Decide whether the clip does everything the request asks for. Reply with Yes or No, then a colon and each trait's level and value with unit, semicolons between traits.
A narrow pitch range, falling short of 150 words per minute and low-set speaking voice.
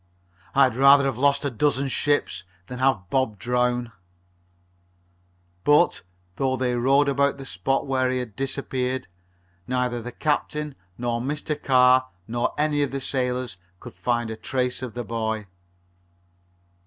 Yes: narrow, 2.1 semitones; average, 140 wpm; low, 130 Hz